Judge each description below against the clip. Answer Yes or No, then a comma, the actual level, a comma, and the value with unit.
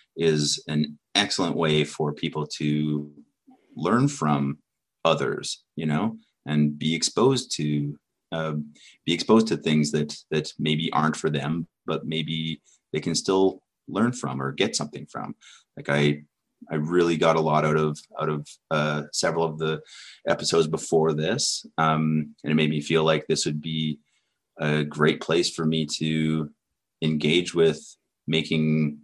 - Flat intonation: Yes, narrow, 1.3 semitones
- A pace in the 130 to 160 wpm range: Yes, average, 155 wpm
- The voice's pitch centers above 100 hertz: No, very low, 75 Hz